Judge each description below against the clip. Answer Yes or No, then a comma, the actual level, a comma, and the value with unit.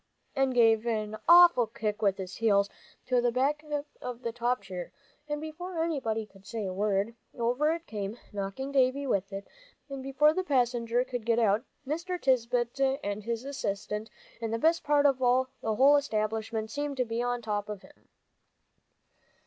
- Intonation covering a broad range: No, average, 4.2 semitones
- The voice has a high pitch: Yes, high, 240 Hz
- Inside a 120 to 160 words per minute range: No, average, 175 wpm